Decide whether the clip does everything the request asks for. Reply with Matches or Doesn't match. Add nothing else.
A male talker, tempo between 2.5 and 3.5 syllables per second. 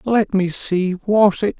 Matches